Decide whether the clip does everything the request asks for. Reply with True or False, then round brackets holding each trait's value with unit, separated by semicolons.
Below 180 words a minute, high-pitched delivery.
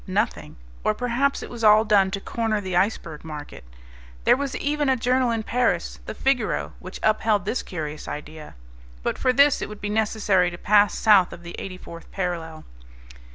False (185 wpm; 210 Hz)